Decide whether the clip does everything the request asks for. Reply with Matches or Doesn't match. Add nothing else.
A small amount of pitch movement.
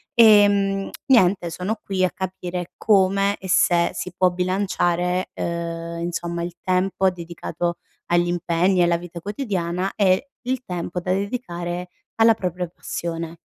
Matches